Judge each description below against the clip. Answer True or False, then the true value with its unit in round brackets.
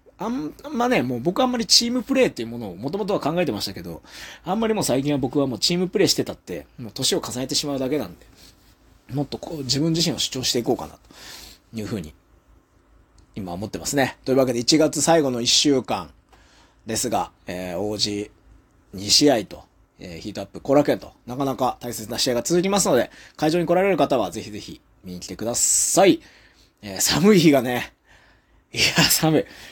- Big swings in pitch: True (8.1 semitones)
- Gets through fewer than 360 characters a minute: False (380 characters per minute)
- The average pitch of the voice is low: True (130 Hz)